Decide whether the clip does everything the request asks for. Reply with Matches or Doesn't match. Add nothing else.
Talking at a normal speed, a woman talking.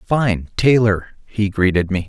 Doesn't match